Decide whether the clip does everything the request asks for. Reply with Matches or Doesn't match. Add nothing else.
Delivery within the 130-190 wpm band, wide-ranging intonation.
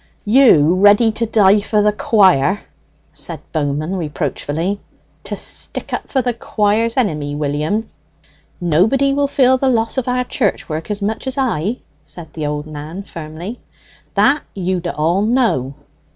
Matches